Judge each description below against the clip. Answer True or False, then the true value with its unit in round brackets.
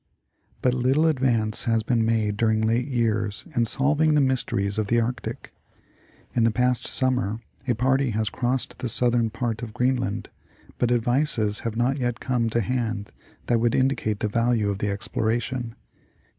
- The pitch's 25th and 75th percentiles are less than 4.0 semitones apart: True (2.4 semitones)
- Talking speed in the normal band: True (165 wpm)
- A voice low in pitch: True (120 Hz)